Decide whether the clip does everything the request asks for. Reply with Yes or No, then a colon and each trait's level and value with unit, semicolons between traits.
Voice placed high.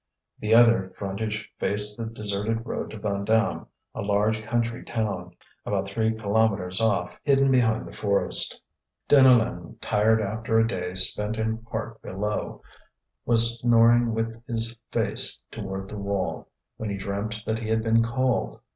No: low, 110 Hz